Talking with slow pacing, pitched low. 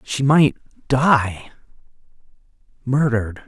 Yes: slow, 70 wpm; low, 130 Hz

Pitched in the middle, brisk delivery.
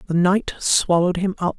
No: medium, 180 Hz; average, 190 wpm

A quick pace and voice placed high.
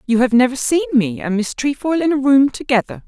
Yes: fast, 235 wpm; very high, 255 Hz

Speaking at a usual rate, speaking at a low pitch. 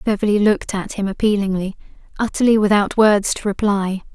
No: average, 145 wpm; high, 205 Hz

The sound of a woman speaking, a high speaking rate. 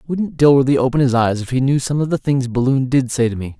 No: male; fast, 285 wpm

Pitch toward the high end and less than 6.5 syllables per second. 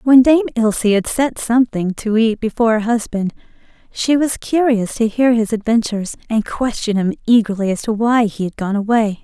Yes: high, 225 Hz; 5.4 syllables/s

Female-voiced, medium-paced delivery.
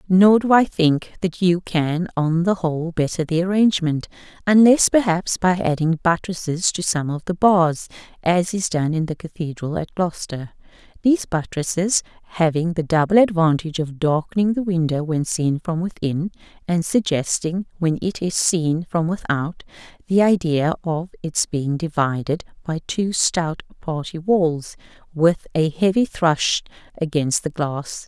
Yes: female; average, 150 wpm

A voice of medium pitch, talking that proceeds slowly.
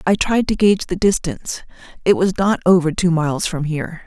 No: medium, 175 Hz; fast, 205 wpm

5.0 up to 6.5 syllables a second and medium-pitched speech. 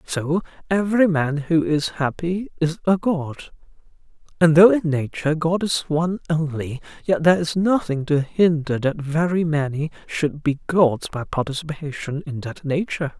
No: 4.7 syllables/s; medium, 160 Hz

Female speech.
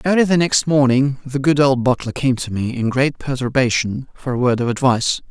No: male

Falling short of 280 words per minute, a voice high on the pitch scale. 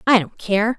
Yes: fast, 230 wpm; high, 215 Hz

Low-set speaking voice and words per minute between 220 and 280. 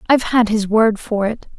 No: high, 220 Hz; fast, 225 wpm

